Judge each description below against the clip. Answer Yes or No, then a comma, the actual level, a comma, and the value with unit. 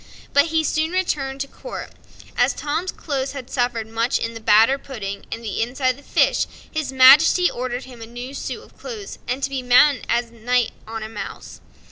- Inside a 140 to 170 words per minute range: No, fast, 205 wpm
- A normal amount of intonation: Yes, average, 3.4 semitones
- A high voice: Yes, very high, 255 Hz